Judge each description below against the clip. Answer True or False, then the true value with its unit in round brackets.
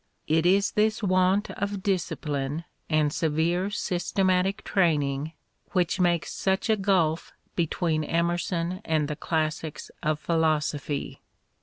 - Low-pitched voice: False (170 Hz)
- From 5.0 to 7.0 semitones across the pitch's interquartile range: False (3.4 semitones)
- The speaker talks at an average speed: False (115 wpm)